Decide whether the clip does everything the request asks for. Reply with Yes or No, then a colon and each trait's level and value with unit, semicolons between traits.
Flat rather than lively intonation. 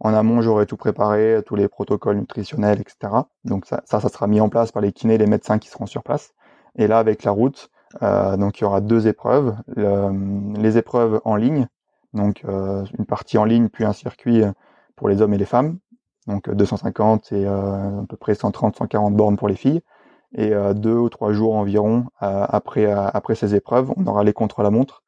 Yes: narrow, 1.8 semitones